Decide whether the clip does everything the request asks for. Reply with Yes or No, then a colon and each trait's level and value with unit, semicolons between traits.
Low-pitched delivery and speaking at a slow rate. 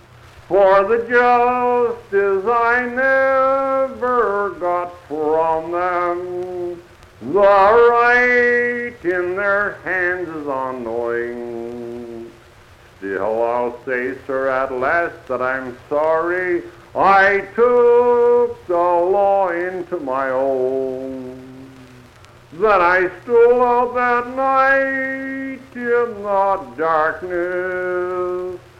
No: medium, 180 Hz; slow, 85 wpm